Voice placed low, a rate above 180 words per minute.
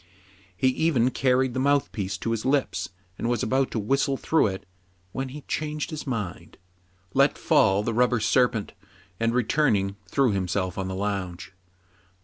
No: low, 120 Hz; average, 160 wpm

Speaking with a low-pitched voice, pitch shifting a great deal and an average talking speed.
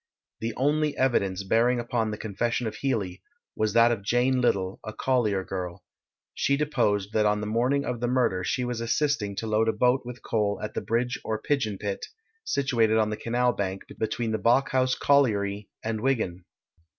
No: low, 115 Hz; average, 3.2 semitones; average, 185 wpm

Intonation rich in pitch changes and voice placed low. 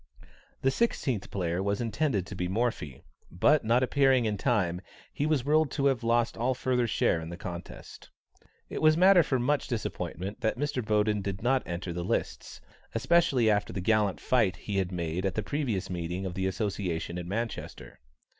Yes: wide, 5.7 semitones; low, 110 Hz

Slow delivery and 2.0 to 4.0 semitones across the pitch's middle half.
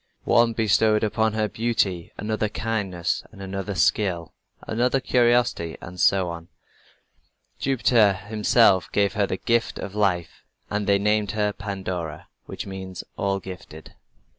Yes: slow, 130 wpm; average, 2.9 semitones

